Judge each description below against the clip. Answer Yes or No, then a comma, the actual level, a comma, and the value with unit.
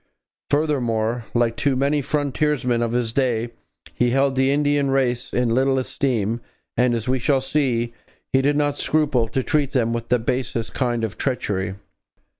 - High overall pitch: No, low, 125 Hz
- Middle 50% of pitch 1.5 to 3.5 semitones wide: Yes, average, 3.0 semitones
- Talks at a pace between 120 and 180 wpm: Yes, average, 165 wpm